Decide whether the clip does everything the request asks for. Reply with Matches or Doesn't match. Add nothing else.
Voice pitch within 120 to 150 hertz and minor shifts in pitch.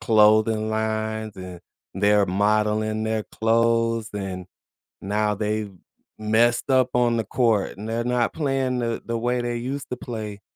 Doesn't match